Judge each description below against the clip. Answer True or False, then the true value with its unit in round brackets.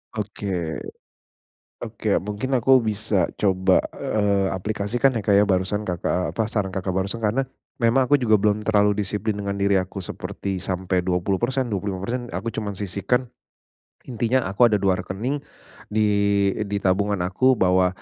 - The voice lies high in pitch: False (100 Hz)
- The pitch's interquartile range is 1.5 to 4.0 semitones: True (2.7 semitones)